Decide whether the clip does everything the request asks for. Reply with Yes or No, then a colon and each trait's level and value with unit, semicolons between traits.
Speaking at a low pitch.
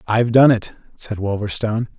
Yes: low, 110 Hz